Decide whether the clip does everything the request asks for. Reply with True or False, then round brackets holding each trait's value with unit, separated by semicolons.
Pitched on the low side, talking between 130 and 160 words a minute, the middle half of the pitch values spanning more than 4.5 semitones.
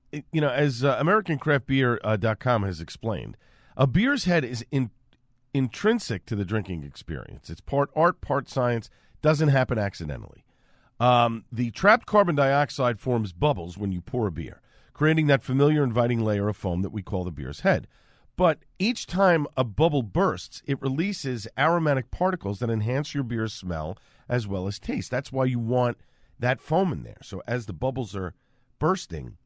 False (125 Hz; 170 wpm; 5.1 semitones)